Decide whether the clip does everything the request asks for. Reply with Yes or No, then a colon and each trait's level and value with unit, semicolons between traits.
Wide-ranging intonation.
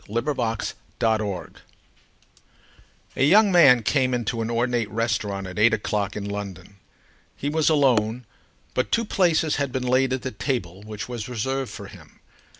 No: average, 3.9 semitones